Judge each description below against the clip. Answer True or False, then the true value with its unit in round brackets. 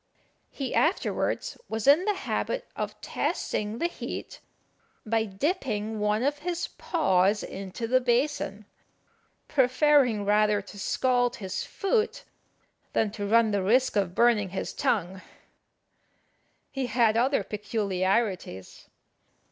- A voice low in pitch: False (225 Hz)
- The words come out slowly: True (115 wpm)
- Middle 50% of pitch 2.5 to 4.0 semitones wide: False (4.8 semitones)